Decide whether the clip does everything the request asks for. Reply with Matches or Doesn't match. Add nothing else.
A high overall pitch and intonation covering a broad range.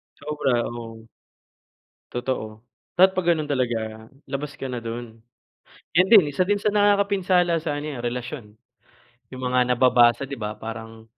Doesn't match